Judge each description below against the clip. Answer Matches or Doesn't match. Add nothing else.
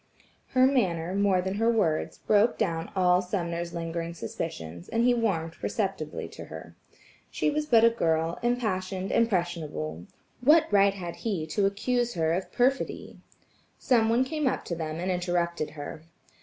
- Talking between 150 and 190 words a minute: Matches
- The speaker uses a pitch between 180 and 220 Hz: Matches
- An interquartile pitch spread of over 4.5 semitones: Matches